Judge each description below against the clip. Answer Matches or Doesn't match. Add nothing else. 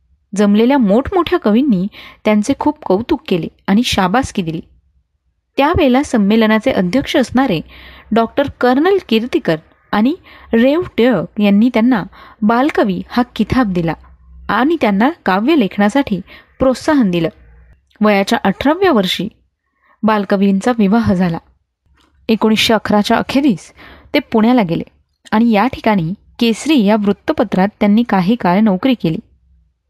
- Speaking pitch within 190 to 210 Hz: Doesn't match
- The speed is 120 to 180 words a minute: Doesn't match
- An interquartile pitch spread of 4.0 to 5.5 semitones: Matches